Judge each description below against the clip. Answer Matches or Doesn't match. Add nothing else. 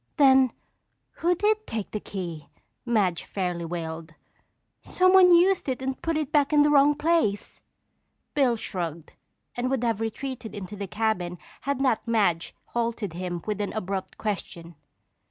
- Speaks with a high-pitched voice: Matches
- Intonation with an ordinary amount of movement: Doesn't match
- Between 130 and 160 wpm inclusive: Matches